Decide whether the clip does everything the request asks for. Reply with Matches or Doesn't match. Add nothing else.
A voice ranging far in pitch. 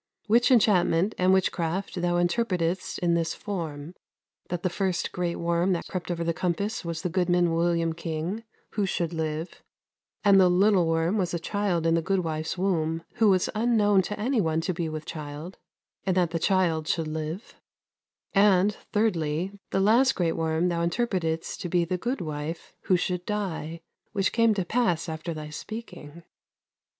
Doesn't match